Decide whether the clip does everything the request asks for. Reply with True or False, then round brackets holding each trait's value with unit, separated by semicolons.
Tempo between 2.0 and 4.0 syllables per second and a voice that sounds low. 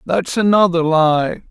False (3.7 syllables/s; 175 Hz)